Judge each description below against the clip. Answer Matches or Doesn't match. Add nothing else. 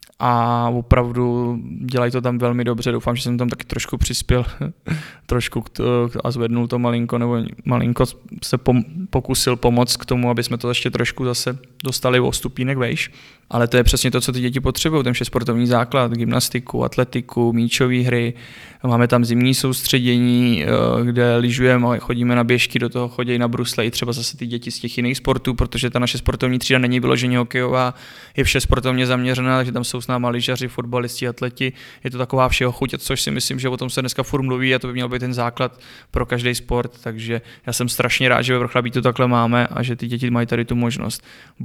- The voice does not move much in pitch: Matches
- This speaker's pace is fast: Matches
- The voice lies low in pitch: Matches